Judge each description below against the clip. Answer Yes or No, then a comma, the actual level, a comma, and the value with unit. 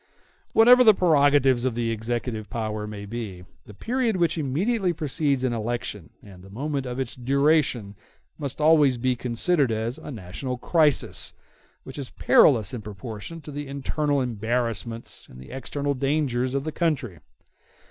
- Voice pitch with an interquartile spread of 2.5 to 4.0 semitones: No, average, 4.6 semitones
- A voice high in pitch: No, low, 130 Hz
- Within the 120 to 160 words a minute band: Yes, average, 155 wpm